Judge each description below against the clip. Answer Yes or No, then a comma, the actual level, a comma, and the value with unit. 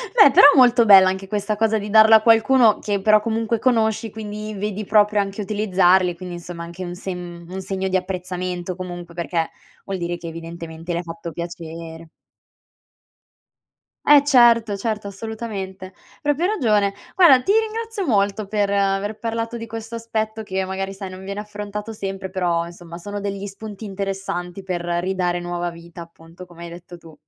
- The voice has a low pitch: No, high, 195 Hz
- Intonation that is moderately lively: Yes, average, 3.6 semitones